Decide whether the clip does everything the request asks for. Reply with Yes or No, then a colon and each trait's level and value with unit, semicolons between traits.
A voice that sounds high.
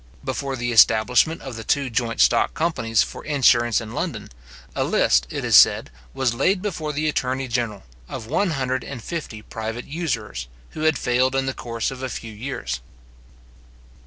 No: low, 125 Hz